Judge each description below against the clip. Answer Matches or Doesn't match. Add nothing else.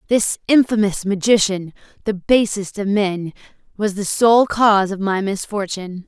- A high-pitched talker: Matches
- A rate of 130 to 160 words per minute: Matches